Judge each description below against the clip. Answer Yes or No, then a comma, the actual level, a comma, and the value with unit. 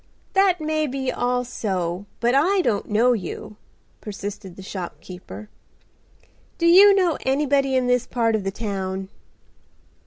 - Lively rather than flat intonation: Yes, wide, 6.2 semitones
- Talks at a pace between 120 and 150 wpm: Yes, slow, 135 wpm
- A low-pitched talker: No, high, 240 Hz